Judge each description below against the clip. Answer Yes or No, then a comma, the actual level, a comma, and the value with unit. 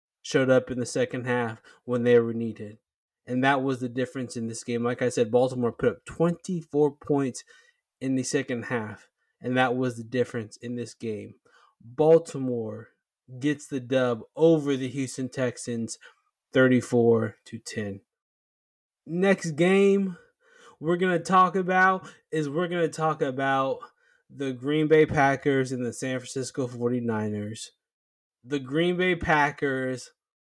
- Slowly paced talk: No, average, 150 wpm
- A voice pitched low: Yes, low, 130 Hz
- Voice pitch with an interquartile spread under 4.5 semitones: No, average, 4.8 semitones